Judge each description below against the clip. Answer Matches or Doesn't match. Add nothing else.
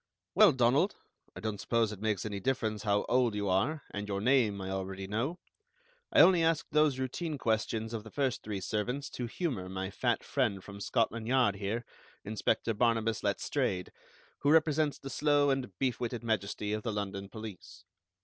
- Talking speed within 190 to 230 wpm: Doesn't match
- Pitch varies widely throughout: Doesn't match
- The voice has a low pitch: Matches